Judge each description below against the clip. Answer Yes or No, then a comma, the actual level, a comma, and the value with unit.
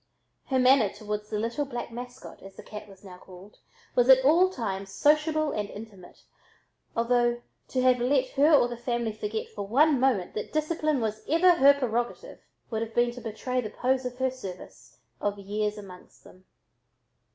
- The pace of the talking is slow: No, average, 175 wpm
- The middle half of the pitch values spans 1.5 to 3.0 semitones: No, average, 4.0 semitones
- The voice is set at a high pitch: Yes, high, 240 Hz